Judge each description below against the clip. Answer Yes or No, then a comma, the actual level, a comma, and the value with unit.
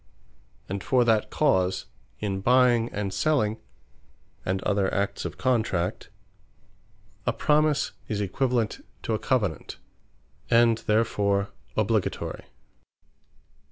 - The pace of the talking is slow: Yes, slow, 100 wpm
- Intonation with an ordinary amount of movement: Yes, average, 3.5 semitones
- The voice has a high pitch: No, low, 110 Hz